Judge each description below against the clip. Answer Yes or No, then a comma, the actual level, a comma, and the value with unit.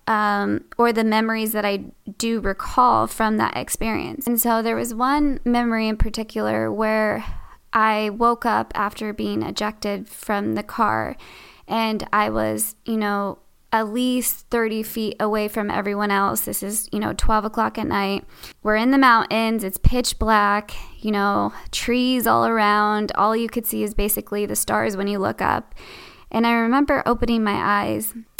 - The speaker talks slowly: No, average, 170 wpm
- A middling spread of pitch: No, narrow, 2.0 semitones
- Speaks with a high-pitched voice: Yes, high, 220 Hz